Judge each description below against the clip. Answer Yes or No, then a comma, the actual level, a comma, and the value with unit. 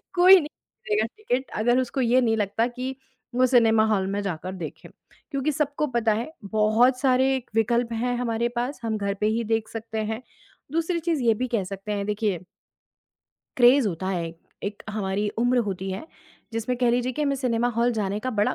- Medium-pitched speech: No, high, 230 Hz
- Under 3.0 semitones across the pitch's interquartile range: No, average, 3.3 semitones